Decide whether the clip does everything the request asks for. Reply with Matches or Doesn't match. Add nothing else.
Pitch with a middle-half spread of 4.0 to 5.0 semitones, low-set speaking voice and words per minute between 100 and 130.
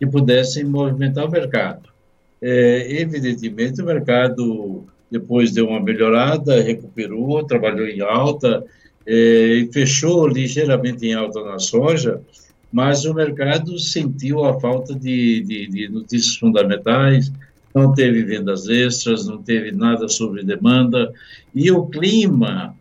Matches